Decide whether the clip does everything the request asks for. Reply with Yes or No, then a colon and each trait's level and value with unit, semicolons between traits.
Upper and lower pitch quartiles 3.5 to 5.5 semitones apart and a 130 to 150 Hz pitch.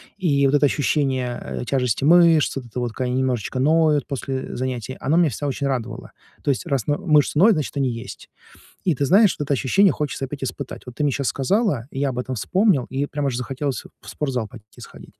No: average, 3.0 semitones; low, 135 Hz